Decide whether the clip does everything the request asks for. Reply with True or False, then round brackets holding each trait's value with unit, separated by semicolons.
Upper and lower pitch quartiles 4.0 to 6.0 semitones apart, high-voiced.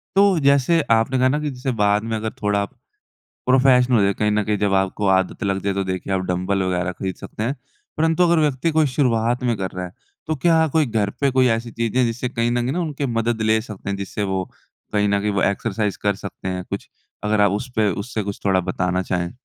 False (4.6 semitones; 110 Hz)